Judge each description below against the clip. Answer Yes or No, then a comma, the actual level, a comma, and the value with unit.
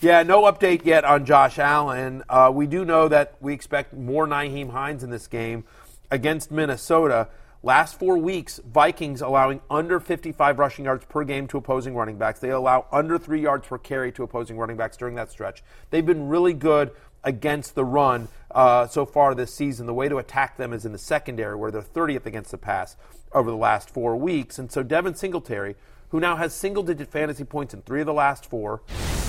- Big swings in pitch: No, average, 3.8 semitones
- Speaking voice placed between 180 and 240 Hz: No, medium, 140 Hz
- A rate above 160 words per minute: Yes, fast, 205 wpm